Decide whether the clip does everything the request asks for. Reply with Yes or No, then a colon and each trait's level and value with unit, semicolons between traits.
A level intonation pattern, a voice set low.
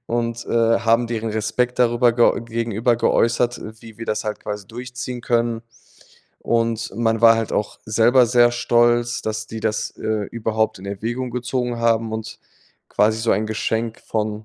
Yes: narrow, 1.4 semitones; low, 115 Hz